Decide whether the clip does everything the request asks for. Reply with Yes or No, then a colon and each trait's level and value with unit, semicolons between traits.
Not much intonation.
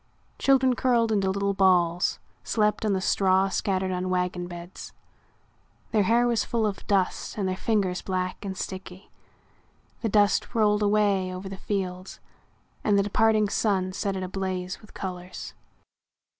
Yes: narrow, 2.3 semitones